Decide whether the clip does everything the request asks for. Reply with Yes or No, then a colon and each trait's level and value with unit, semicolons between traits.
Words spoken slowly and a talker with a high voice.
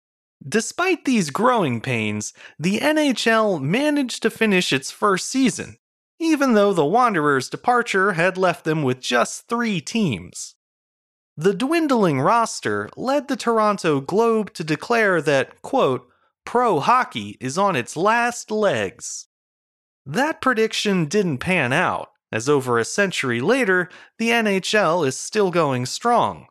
Yes: slow, 130 wpm; high, 205 Hz